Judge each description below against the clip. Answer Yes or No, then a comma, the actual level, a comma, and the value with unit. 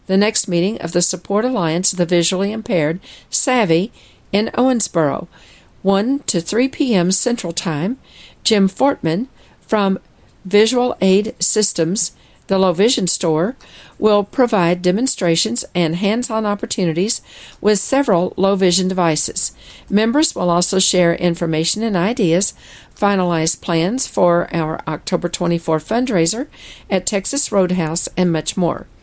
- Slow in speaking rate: Yes, slow, 125 wpm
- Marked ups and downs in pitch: No, average, 4.1 semitones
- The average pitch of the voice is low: No, high, 190 Hz